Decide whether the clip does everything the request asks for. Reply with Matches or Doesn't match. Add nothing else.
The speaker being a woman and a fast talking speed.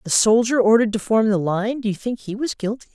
Matches